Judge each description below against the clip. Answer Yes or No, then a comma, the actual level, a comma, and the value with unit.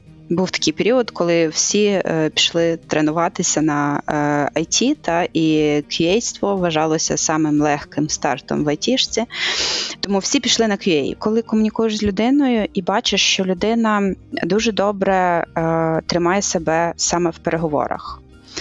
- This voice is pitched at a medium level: Yes, medium, 175 Hz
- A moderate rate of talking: Yes, average, 130 wpm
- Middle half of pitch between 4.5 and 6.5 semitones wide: Yes, average, 5.1 semitones